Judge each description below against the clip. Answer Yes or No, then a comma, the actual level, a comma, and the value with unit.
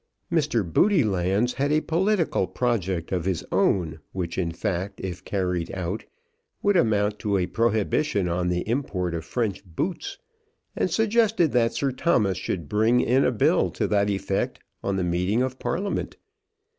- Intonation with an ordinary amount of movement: No, wide, 6.1 semitones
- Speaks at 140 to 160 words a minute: Yes, average, 155 wpm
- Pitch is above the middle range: No, low, 105 Hz